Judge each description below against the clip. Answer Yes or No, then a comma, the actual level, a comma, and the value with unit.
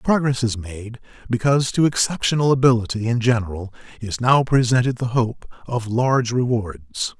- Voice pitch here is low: Yes, low, 120 Hz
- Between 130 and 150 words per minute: Yes, average, 140 wpm